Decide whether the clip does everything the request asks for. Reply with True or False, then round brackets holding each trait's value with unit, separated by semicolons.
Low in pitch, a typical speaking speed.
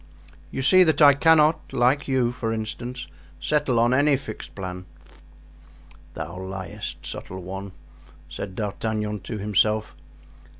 False (115 Hz; 125 wpm)